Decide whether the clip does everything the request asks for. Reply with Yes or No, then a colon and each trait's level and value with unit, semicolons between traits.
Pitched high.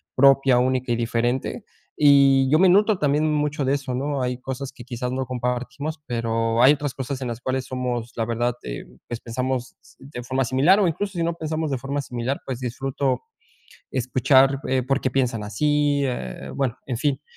No: low, 130 Hz